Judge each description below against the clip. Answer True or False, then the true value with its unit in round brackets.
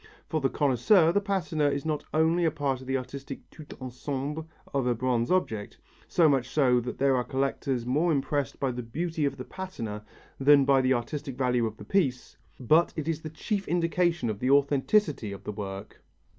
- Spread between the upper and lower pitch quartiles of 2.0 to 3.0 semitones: False (4.1 semitones)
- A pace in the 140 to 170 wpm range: False (200 wpm)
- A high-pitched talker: False (140 Hz)